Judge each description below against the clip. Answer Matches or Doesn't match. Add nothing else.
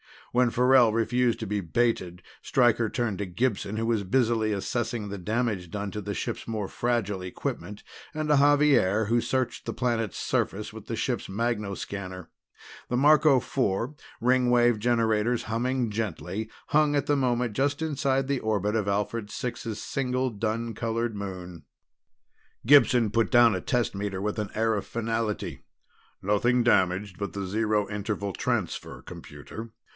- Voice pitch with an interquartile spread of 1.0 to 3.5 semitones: Matches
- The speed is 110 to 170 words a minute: Matches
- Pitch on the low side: Matches